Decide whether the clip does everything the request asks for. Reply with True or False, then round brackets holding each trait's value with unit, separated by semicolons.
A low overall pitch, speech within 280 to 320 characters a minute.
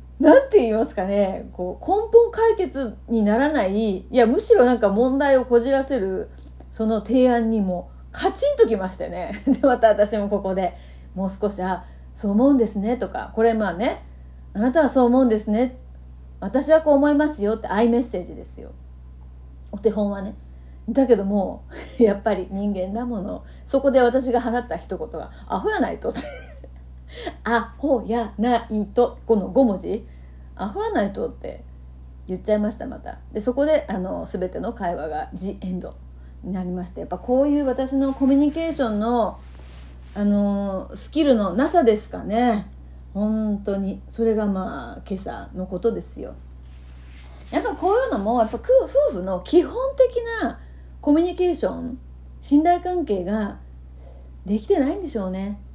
False (215 Hz; 310 characters per minute)